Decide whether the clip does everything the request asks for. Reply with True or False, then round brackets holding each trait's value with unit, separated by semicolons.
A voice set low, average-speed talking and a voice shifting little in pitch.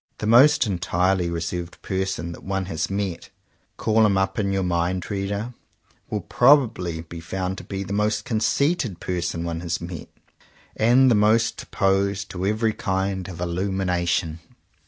False (95 Hz; 160 wpm; 3.2 semitones)